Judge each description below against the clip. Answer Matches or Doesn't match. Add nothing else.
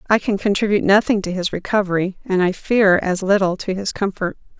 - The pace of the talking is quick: Doesn't match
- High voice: Matches